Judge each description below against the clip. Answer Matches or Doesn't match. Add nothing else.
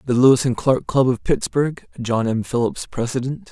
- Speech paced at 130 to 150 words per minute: Doesn't match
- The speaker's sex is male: Matches